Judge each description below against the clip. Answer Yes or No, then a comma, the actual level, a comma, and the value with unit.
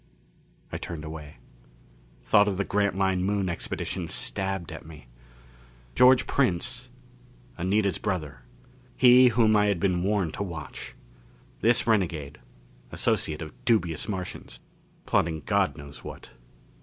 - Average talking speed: No, slow, 120 wpm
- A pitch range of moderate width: Yes, average, 4.4 semitones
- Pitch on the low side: Yes, very low, 95 Hz